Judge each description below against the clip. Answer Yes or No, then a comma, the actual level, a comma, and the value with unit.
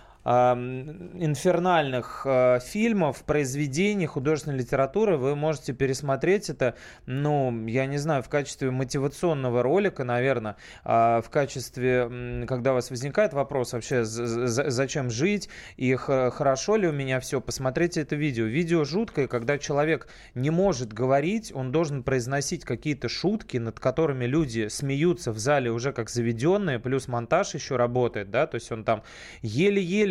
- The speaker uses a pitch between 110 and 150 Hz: Yes, low, 135 Hz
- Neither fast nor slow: Yes, average, 135 wpm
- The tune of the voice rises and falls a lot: No, average, 4.3 semitones